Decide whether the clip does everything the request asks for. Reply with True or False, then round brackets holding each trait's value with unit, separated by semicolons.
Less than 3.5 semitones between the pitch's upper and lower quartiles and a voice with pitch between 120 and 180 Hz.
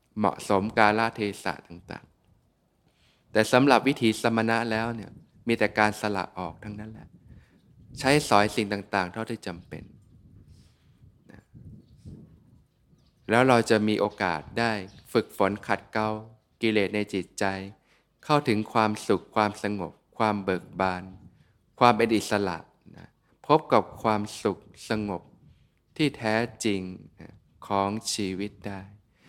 False (2.4 semitones; 105 Hz)